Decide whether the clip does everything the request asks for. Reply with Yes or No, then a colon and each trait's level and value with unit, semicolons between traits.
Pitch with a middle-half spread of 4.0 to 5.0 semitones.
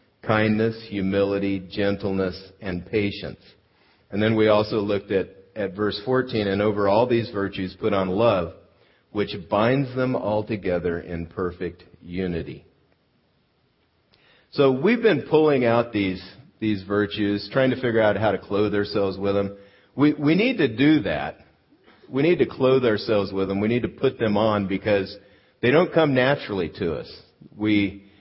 No: average, 3.3 semitones